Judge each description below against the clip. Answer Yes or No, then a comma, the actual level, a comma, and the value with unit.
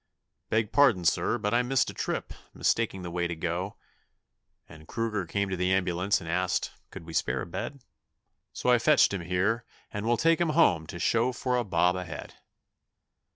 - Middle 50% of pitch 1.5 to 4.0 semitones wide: No, wide, 5.4 semitones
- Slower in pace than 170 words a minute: No, average, 195 wpm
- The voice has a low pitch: Yes, low, 100 Hz